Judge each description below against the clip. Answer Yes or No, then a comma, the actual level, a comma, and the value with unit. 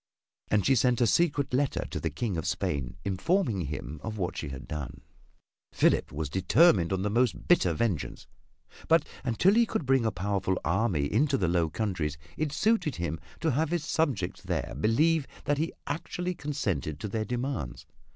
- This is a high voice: No, low, 110 Hz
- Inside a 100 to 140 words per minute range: No, average, 180 wpm